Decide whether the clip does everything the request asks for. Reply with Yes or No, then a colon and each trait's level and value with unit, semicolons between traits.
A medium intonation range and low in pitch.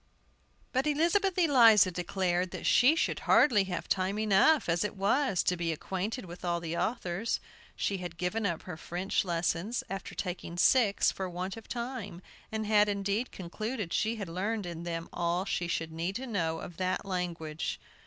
No: average, 4.1 semitones; high, 190 Hz